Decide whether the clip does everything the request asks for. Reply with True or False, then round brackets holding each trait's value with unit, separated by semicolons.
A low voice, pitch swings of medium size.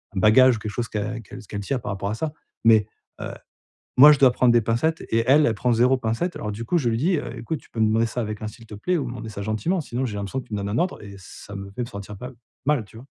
True (115 Hz; 3.5 semitones)